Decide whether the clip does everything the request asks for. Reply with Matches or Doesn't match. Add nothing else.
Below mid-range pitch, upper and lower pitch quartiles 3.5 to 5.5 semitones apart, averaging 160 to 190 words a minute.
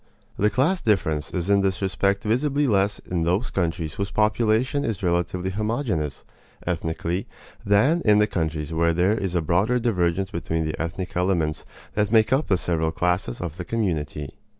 Matches